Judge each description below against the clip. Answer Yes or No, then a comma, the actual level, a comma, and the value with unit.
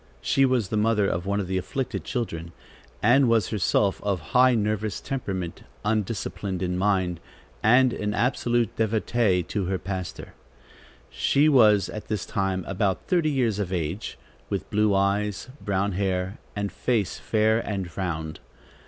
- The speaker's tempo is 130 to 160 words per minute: Yes, average, 150 wpm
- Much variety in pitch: No, average, 3.2 semitones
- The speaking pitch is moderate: No, low, 105 Hz